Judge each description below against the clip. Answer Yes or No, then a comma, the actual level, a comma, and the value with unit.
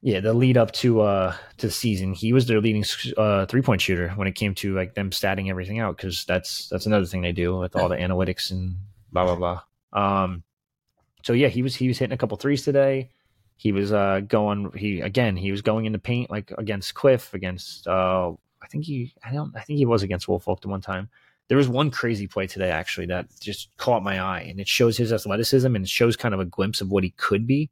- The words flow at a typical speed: No, fast, 240 wpm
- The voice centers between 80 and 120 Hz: Yes, low, 105 Hz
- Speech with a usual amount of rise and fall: Yes, average, 4.1 semitones